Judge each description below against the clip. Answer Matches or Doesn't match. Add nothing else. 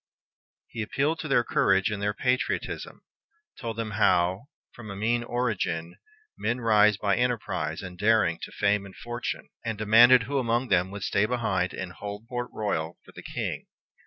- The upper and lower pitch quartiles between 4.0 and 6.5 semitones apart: Doesn't match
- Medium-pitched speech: Doesn't match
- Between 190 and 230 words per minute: Doesn't match